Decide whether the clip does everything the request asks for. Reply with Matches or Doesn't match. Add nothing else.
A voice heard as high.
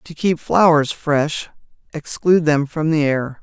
Doesn't match